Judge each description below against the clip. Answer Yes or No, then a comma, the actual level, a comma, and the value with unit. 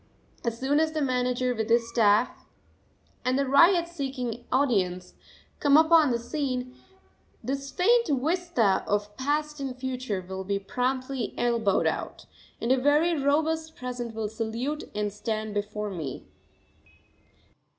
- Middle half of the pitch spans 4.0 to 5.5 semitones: Yes, average, 4.7 semitones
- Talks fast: No, slow, 135 wpm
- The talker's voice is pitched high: Yes, very high, 255 Hz